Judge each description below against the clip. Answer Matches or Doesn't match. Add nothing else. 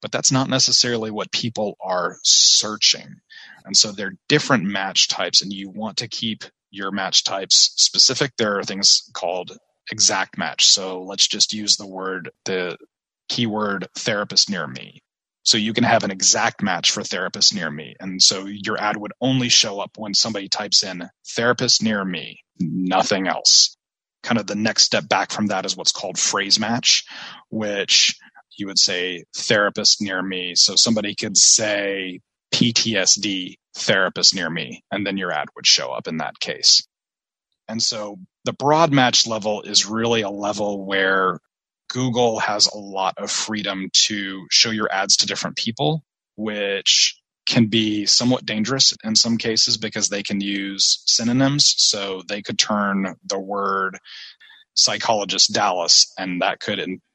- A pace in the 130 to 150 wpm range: Doesn't match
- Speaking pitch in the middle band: Doesn't match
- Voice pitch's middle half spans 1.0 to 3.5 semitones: Matches